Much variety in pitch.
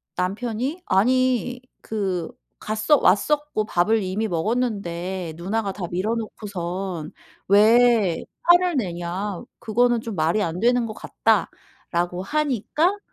No: average, 5.0 semitones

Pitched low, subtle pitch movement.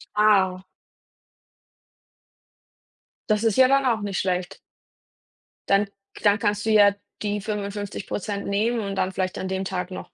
No: high, 205 Hz; narrow, 1.9 semitones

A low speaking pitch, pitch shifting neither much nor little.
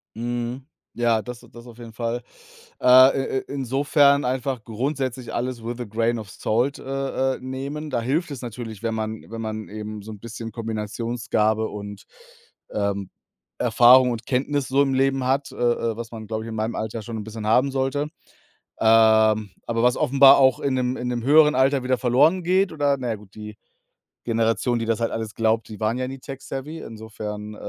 Yes: low, 120 Hz; average, 3.2 semitones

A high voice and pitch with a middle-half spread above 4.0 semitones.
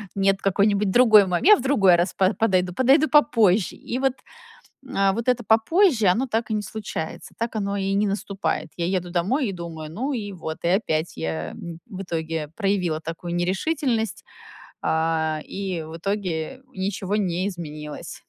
Yes: high, 195 Hz; average, 4.5 semitones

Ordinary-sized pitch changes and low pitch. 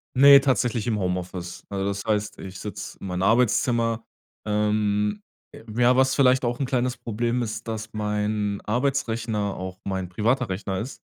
Yes: average, 3.2 semitones; low, 110 Hz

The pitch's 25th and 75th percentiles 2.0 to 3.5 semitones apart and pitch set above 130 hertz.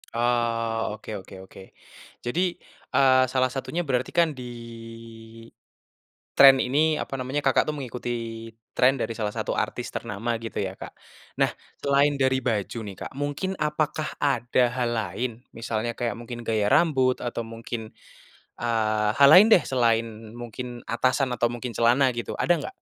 No: average, 3.0 semitones; low, 120 Hz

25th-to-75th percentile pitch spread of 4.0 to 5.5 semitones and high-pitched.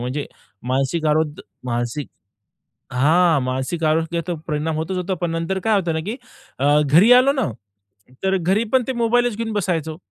No: average, 5.2 semitones; medium, 165 Hz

